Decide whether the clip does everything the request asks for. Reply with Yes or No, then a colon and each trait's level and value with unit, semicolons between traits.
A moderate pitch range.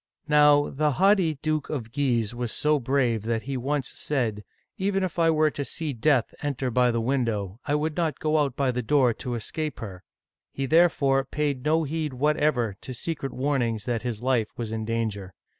Yes: average, 4.4 semitones